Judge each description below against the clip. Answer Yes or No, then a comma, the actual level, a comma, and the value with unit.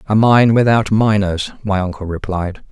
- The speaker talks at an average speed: Yes, average, 155 wpm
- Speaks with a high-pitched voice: No, low, 100 Hz